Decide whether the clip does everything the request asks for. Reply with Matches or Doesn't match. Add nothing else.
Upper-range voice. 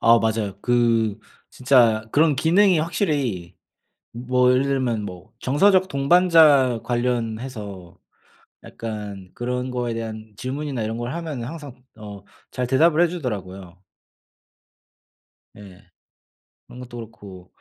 Doesn't match